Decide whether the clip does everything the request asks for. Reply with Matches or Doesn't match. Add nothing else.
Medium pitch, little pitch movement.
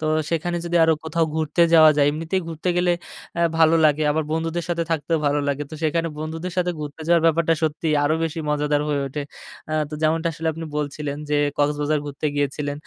Matches